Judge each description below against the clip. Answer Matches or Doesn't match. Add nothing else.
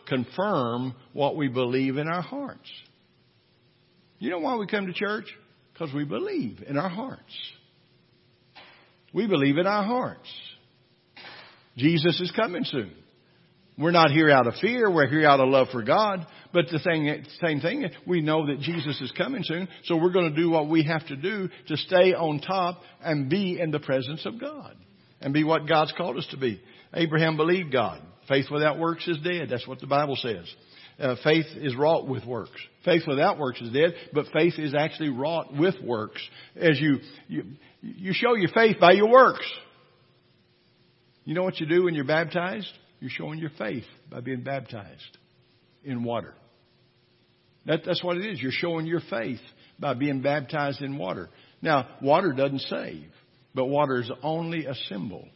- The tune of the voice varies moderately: Matches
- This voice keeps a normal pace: Matches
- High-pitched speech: Doesn't match